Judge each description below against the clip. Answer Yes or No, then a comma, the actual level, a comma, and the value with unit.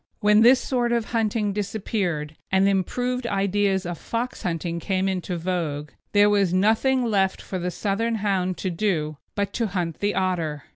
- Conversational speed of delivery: Yes, average, 165 wpm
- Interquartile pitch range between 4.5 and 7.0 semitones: No, average, 3.3 semitones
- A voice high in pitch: Yes, high, 195 Hz